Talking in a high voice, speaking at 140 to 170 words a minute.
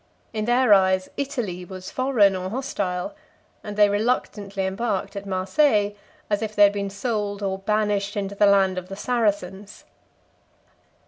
Yes: high, 205 Hz; average, 150 wpm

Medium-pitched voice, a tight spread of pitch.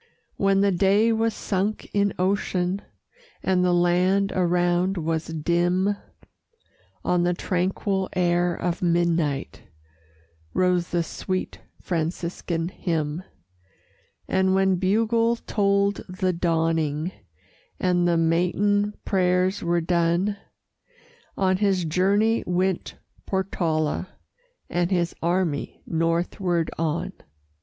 Yes: medium, 180 Hz; narrow, 2.1 semitones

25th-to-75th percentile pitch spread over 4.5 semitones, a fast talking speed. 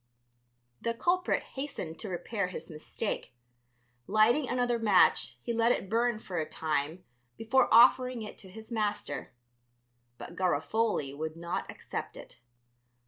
No: average, 5.2 semitones; slow, 135 wpm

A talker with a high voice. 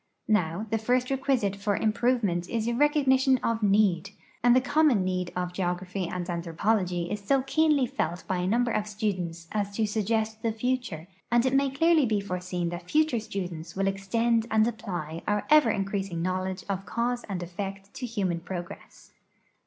Yes: high, 205 Hz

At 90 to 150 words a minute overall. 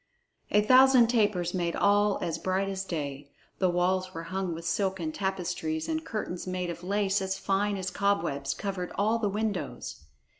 No: average, 165 wpm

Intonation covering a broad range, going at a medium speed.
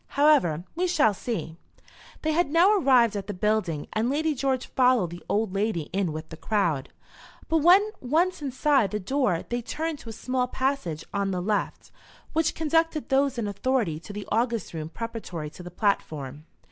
Yes: wide, 7.6 semitones; average, 180 wpm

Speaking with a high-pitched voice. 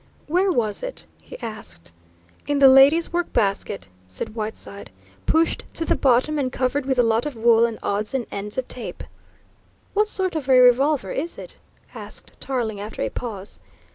Yes: very high, 250 Hz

